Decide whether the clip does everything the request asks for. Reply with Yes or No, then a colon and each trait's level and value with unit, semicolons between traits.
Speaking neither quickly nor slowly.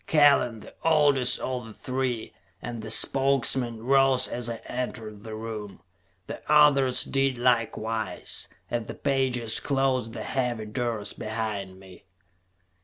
No: slow, 130 wpm